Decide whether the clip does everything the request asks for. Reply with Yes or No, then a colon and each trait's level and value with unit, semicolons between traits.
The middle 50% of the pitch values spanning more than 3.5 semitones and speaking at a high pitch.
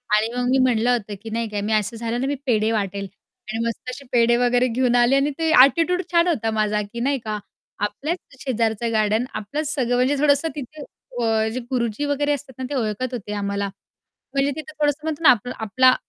Yes: average, 4.1 semitones; high, 245 Hz